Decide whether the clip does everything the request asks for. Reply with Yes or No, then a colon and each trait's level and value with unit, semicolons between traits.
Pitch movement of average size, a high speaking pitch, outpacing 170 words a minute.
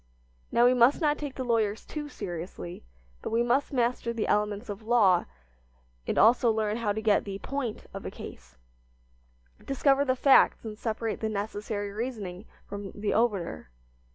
No: average, 3.2 semitones; high, 220 Hz; average, 165 wpm